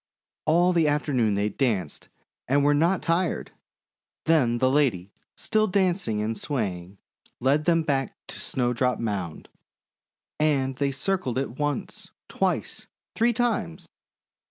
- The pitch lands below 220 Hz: Yes, low, 135 Hz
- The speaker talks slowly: Yes, slow, 130 wpm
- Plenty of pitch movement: Yes, wide, 6.2 semitones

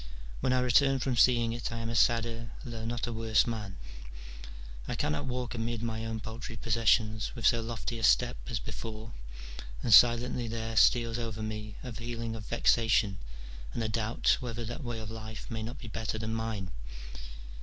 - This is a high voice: No, low, 115 Hz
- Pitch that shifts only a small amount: Yes, narrow, 1.2 semitones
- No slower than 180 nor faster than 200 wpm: Yes, average, 185 wpm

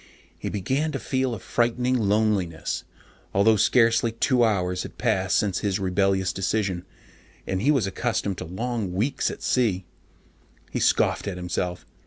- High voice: No, low, 100 Hz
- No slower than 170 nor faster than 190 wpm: No, average, 155 wpm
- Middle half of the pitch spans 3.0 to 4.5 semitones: Yes, average, 4.2 semitones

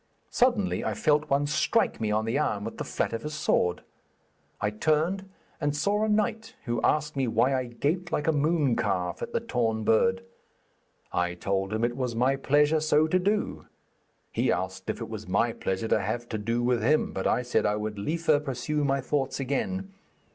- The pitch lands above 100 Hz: Yes, low, 135 Hz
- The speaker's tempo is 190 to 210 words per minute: Yes, average, 200 wpm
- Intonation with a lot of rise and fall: Yes, wide, 5.7 semitones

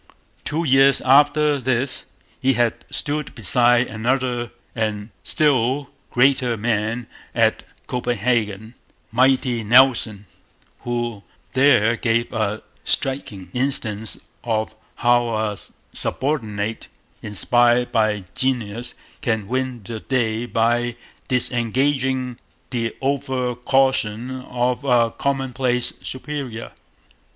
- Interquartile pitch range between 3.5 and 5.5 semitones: No, average, 2.8 semitones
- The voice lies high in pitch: No, low, 120 Hz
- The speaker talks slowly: Yes, slow, 95 wpm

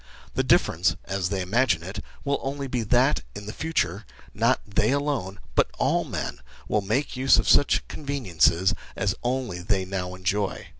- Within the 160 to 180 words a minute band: Yes, average, 165 wpm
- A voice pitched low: Yes, low, 105 Hz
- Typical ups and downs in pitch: No, wide, 5.9 semitones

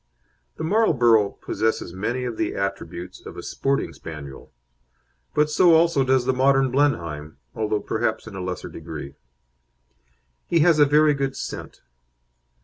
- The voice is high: No, low, 120 Hz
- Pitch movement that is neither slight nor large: No, wide, 7.2 semitones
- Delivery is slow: No, average, 145 wpm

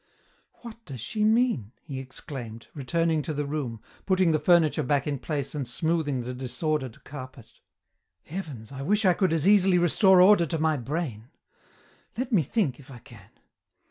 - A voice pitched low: No, medium, 150 Hz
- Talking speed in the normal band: Yes, average, 170 wpm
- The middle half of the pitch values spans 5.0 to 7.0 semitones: Yes, average, 5.3 semitones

